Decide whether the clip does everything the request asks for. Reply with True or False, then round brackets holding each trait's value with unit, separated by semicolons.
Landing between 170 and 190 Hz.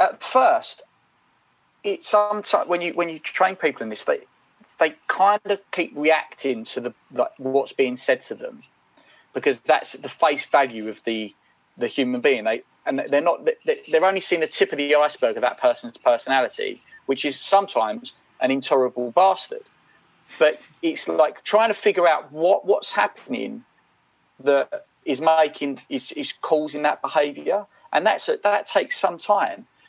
True (185 Hz)